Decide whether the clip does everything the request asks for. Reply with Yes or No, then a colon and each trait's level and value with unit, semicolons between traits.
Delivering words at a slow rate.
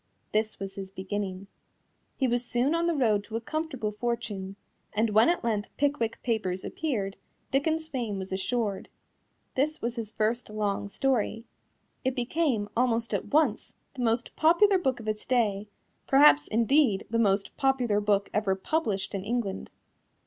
No: average, 155 wpm